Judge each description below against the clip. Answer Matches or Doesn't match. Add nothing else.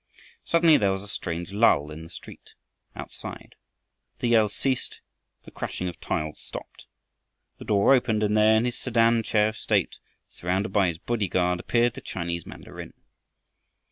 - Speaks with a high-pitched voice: Doesn't match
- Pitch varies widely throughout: Doesn't match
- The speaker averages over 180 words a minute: Doesn't match